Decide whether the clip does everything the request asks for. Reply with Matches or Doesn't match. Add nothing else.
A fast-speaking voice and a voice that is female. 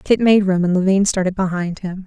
Matches